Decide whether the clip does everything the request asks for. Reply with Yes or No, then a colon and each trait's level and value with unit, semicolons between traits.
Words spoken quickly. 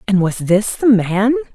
No: average, 195 wpm